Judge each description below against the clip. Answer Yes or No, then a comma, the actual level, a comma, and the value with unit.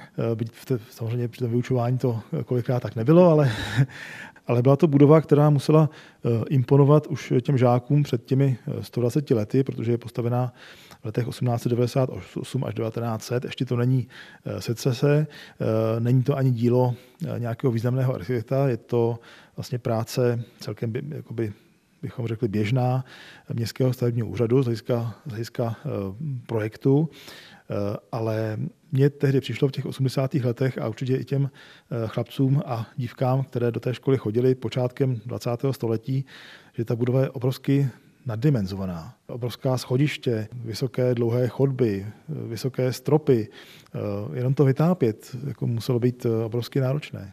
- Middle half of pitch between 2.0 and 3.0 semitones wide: Yes, average, 2.7 semitones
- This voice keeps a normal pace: Yes, average, 135 wpm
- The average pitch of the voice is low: Yes, low, 125 Hz